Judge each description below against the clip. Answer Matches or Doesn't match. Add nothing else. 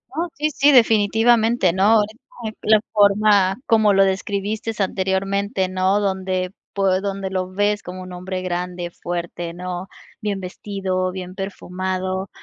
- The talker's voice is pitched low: Doesn't match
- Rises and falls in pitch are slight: Matches